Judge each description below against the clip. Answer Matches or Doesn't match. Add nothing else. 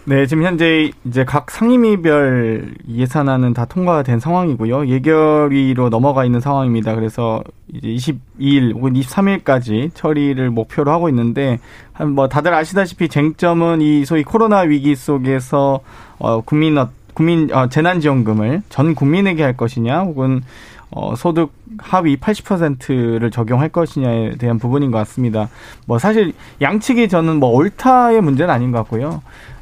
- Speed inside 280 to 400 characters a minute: Matches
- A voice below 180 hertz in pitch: Matches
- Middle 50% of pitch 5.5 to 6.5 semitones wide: Doesn't match